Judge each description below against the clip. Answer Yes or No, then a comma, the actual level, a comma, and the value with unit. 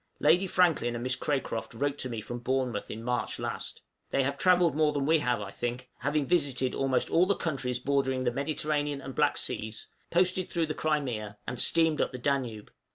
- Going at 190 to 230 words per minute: Yes, average, 200 wpm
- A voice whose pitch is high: No, low, 135 Hz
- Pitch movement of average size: Yes, average, 3.8 semitones